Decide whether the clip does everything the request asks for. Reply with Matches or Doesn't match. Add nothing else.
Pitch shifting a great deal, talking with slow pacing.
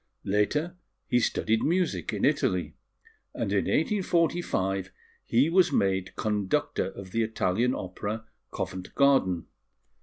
Matches